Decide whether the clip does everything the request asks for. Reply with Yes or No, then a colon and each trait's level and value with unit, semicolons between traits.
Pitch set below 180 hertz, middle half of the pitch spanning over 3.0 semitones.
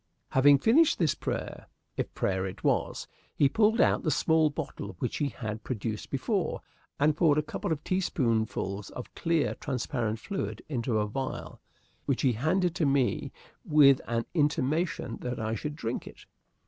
Yes: medium, 140 Hz; wide, 5.4 semitones